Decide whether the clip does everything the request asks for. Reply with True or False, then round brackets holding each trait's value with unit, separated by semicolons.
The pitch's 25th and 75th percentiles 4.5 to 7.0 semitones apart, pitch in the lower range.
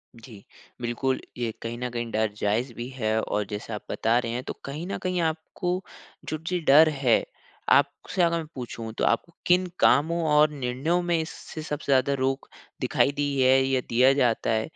True (5.0 semitones; 130 Hz)